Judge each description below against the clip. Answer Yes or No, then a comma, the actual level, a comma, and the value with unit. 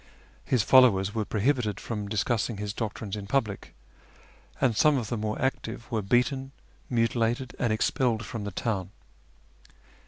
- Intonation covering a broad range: No, average, 3.0 semitones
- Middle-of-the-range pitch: No, low, 115 Hz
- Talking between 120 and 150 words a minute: Yes, average, 145 wpm